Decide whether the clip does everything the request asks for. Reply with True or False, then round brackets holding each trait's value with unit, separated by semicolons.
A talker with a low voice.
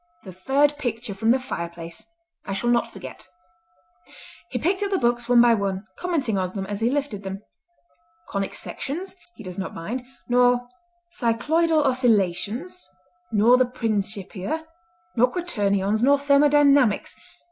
False (240 Hz)